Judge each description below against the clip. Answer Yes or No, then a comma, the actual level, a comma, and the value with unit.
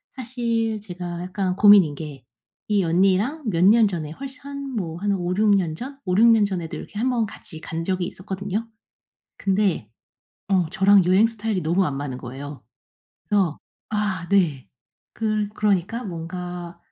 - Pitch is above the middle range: Yes, high, 195 Hz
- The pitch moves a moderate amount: Yes, average, 3.8 semitones